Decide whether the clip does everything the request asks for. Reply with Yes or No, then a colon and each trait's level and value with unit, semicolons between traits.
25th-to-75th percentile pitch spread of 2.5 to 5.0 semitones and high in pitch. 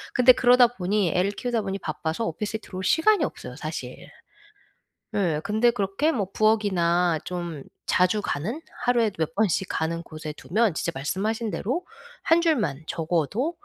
No: wide, 5.5 semitones; high, 200 Hz